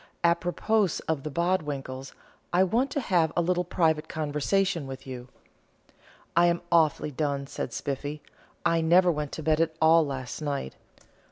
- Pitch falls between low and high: Yes, medium, 160 Hz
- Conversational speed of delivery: Yes, average, 155 wpm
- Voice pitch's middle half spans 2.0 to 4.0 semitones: Yes, average, 3.4 semitones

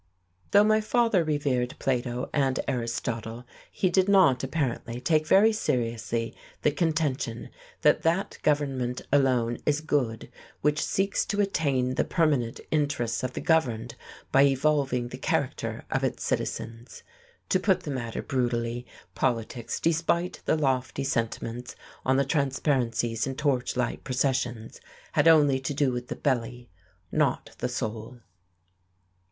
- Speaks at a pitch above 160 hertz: No, low, 130 Hz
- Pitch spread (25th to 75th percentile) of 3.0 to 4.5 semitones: Yes, average, 4.1 semitones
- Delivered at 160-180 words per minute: No, slow, 135 wpm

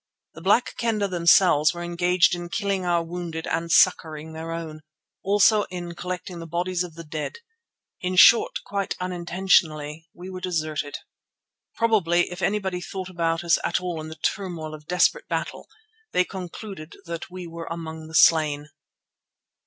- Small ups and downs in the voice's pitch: Yes, narrow, 2.2 semitones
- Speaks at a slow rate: No, average, 155 wpm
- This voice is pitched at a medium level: Yes, medium, 175 Hz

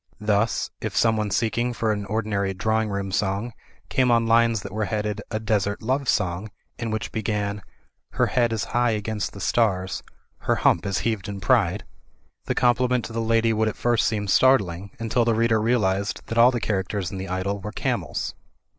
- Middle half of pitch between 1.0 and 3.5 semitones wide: Yes, narrow, 2.5 semitones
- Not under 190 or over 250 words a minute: Yes, average, 195 wpm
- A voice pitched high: No, low, 110 Hz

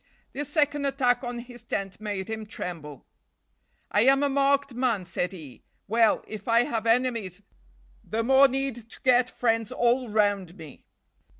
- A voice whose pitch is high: Yes, high, 235 Hz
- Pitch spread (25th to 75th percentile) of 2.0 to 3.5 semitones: No, average, 4.2 semitones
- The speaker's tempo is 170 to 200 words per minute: No, average, 160 wpm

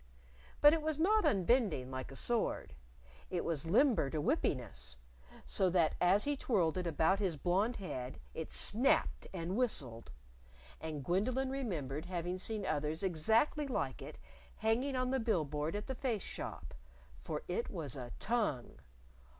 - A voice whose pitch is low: No, medium, 185 Hz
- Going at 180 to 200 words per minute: No, average, 155 wpm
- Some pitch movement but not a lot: No, wide, 7.8 semitones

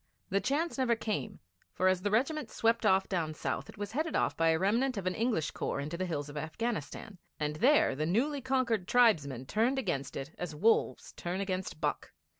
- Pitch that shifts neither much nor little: No, wide, 6.9 semitones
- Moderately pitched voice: No, high, 195 Hz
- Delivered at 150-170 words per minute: No, fast, 205 wpm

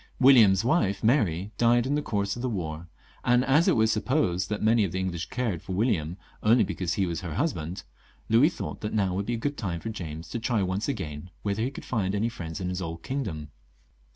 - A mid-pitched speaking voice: No, low, 100 Hz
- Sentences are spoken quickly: Yes, fast, 235 wpm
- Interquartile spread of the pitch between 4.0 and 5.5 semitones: Yes, average, 5.0 semitones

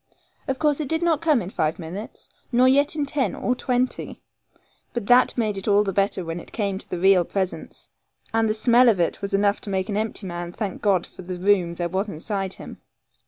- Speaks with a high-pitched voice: Yes, high, 205 Hz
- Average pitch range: Yes, average, 4.8 semitones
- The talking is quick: Yes, fast, 225 wpm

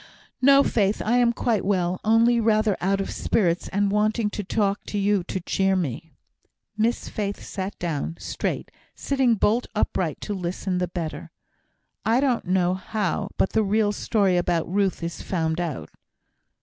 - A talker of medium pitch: No, high, 200 Hz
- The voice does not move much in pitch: No, average, 3.3 semitones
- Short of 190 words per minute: Yes, average, 160 wpm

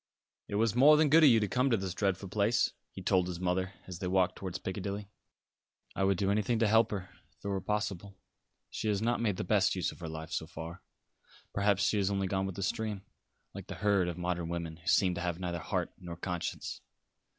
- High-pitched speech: No, very low, 95 Hz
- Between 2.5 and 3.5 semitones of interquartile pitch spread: Yes, average, 2.8 semitones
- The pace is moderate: No, fast, 230 wpm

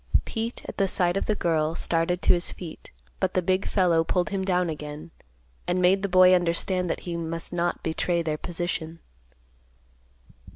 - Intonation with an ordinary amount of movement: No, narrow, 1.8 semitones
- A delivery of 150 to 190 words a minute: Yes, average, 170 wpm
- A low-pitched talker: No, medium, 175 Hz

